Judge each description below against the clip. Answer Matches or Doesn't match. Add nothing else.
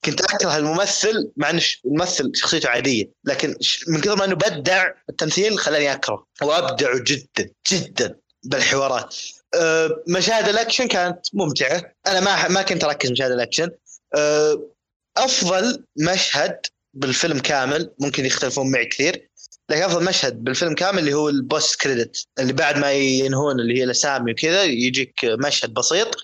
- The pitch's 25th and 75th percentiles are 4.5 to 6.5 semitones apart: Matches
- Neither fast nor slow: Doesn't match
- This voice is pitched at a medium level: Matches